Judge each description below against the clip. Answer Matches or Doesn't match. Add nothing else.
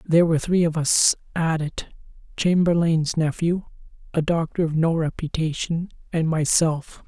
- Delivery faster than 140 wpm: Doesn't match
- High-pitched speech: Doesn't match